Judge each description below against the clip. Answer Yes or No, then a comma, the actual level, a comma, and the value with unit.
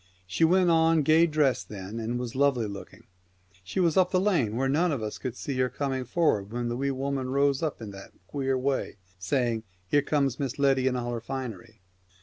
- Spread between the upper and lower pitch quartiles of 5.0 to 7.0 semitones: No, average, 3.9 semitones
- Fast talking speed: Yes, fast, 215 wpm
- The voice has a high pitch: No, low, 135 Hz